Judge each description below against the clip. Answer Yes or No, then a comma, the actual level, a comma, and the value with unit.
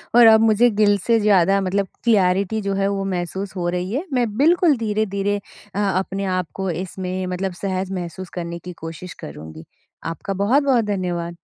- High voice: Yes, high, 195 Hz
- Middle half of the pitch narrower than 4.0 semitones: Yes, average, 2.7 semitones